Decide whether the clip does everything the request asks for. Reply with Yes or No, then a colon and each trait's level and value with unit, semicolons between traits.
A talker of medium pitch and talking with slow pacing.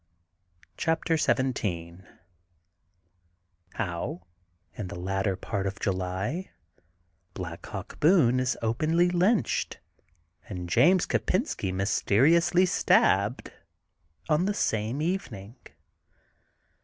No: low, 115 Hz; slow, 85 wpm